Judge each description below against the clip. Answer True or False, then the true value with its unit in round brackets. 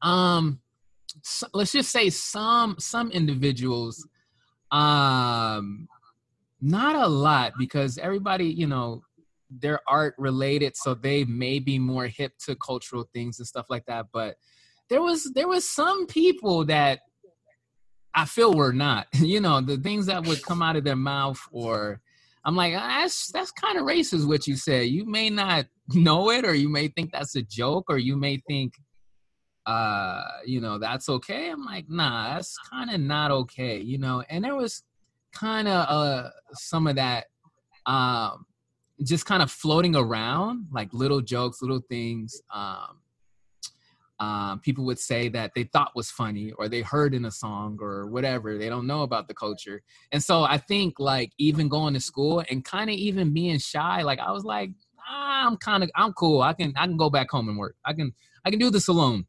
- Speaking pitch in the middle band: True (145 Hz)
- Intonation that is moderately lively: False (5.8 semitones)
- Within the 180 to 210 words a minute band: True (185 wpm)